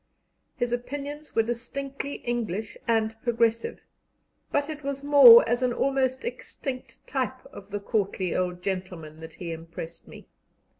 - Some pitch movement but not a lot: No, wide, 5.8 semitones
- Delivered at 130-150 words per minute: Yes, average, 140 wpm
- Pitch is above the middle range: Yes, high, 235 Hz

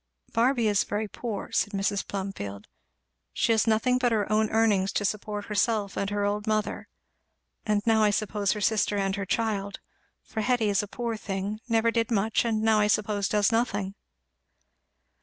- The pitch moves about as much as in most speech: No, narrow, 1.7 semitones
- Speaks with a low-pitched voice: No, high, 210 Hz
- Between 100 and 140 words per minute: No, average, 175 wpm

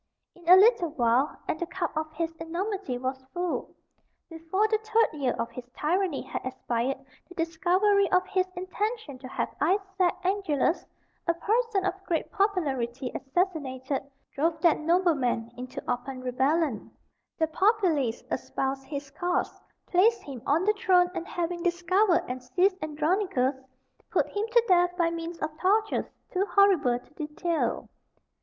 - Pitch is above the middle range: Yes, very high, 335 Hz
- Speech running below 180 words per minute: Yes, average, 150 wpm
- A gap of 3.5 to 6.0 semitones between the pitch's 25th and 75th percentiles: Yes, wide, 5.6 semitones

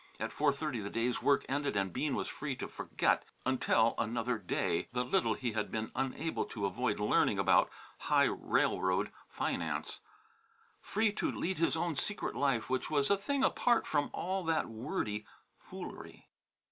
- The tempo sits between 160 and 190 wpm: Yes, average, 165 wpm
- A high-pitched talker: No, low, 135 Hz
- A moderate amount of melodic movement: No, wide, 6.3 semitones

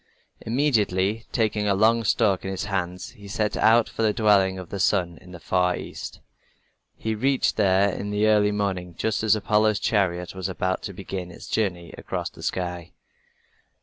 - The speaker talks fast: No, average, 180 wpm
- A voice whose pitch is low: Yes, low, 100 Hz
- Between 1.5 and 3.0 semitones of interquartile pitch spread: Yes, average, 2.7 semitones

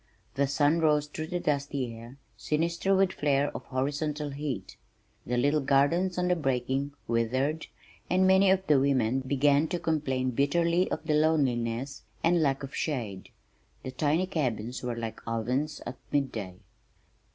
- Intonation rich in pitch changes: No, average, 3.5 semitones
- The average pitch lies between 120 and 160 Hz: Yes, medium, 140 Hz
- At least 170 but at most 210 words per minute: No, average, 155 wpm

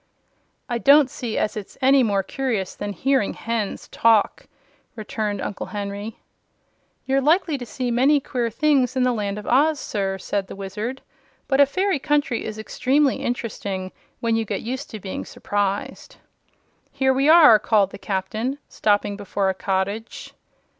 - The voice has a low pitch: No, high, 230 Hz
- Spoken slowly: No, average, 160 wpm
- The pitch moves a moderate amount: Yes, average, 4.7 semitones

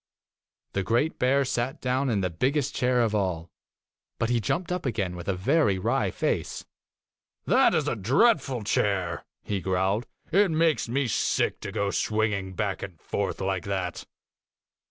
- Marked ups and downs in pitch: Yes, wide, 5.8 semitones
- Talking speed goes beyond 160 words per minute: Yes, average, 170 wpm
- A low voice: Yes, low, 110 Hz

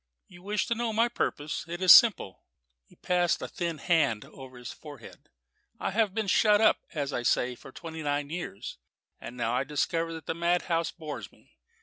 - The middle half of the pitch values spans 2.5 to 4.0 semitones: No, average, 4.8 semitones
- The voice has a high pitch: No, medium, 165 Hz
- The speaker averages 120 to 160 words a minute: No, average, 195 wpm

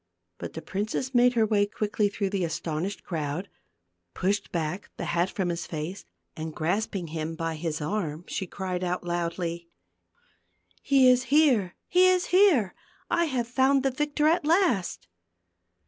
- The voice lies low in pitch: No, high, 195 Hz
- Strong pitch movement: Yes, wide, 7.1 semitones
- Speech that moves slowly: No, average, 155 wpm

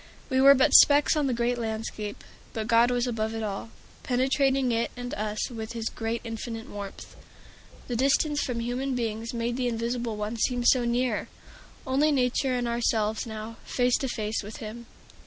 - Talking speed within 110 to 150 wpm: No, average, 175 wpm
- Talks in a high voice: Yes, high, 235 Hz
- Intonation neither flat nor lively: No, narrow, 2.2 semitones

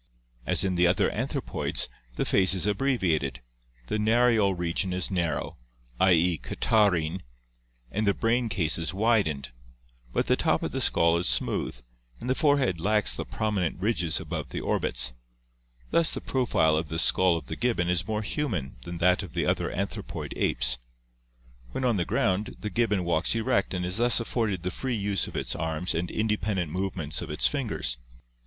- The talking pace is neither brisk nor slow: Yes, average, 175 wpm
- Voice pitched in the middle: No, very low, 95 Hz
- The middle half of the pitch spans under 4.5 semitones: No, average, 4.8 semitones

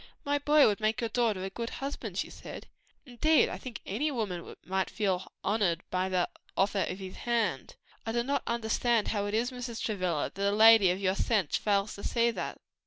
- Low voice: No, high, 215 Hz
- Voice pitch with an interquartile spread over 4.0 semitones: No, average, 3.6 semitones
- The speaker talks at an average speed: No, fast, 215 wpm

